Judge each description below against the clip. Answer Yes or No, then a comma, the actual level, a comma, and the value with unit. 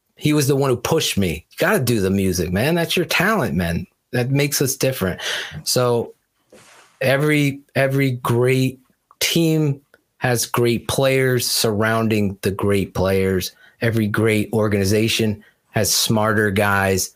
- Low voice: Yes, low, 120 Hz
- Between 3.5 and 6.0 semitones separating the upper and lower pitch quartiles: Yes, average, 5.0 semitones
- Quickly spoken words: No, slow, 135 wpm